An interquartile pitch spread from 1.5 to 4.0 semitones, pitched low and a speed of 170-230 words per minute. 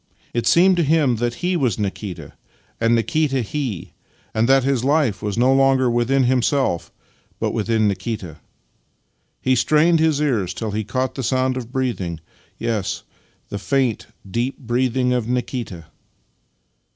No: average, 3.6 semitones; low, 125 Hz; average, 150 wpm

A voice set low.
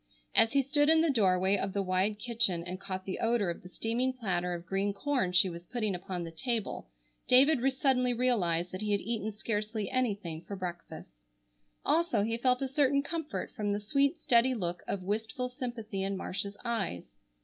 No: high, 210 Hz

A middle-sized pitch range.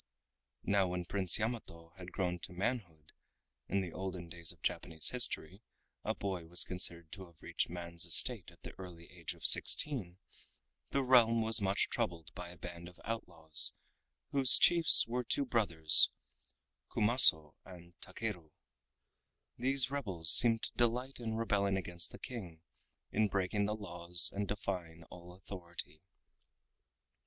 Yes: average, 4.7 semitones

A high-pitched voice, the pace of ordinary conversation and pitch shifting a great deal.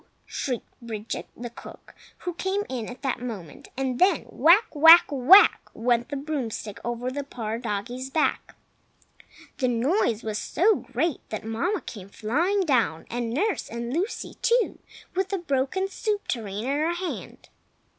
Yes: very high, 260 Hz; average, 150 wpm; wide, 6.9 semitones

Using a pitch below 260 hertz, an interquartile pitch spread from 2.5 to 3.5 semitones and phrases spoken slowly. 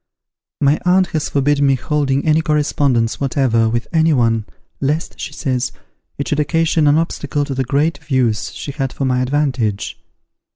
No: medium, 140 Hz; average, 2.9 semitones; average, 165 wpm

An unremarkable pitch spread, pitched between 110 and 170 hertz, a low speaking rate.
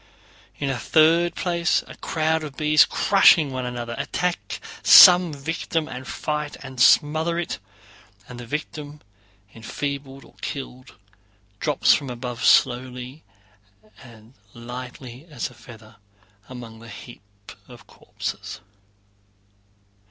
Yes: average, 4.2 semitones; low, 135 Hz; slow, 115 wpm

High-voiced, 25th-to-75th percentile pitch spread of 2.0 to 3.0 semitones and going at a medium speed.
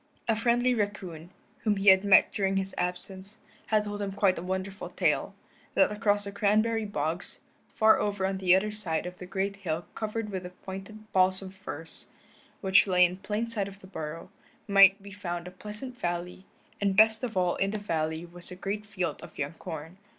Yes: high, 195 Hz; narrow, 2.5 semitones; average, 195 wpm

